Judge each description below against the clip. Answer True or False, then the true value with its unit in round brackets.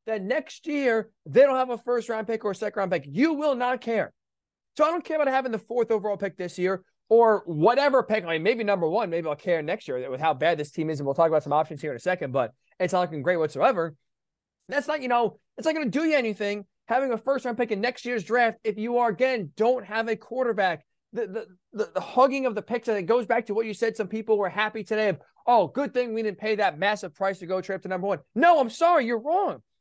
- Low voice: False (220 Hz)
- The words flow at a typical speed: False (270 wpm)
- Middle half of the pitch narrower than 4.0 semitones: False (4.6 semitones)